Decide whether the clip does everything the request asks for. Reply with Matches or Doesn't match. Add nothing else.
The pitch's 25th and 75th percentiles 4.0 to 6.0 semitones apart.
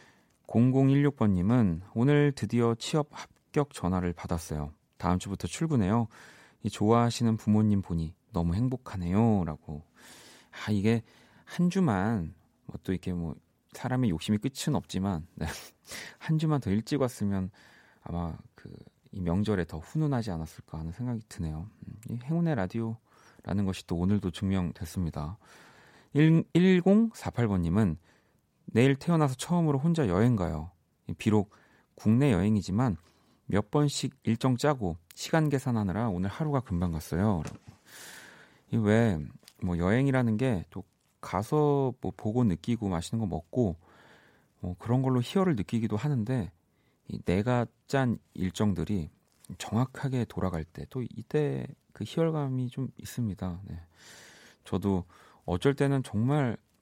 Doesn't match